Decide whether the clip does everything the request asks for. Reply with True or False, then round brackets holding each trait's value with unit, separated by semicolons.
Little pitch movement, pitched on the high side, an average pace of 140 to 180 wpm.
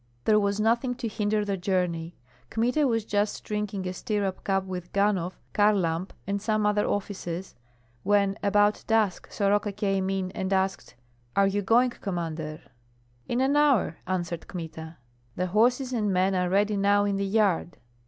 True (2.3 semitones; 200 Hz; 160 wpm)